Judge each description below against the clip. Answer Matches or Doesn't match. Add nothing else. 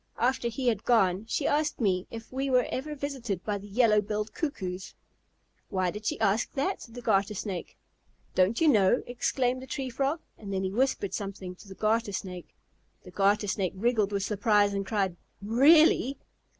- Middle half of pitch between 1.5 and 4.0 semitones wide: Doesn't match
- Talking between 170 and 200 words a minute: Matches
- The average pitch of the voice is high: Matches